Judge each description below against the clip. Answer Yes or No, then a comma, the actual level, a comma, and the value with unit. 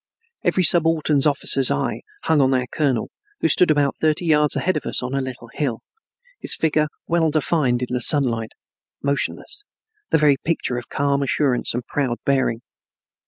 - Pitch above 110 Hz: Yes, medium, 140 Hz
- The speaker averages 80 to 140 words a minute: No, average, 165 wpm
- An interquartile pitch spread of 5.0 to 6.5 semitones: No, average, 3.6 semitones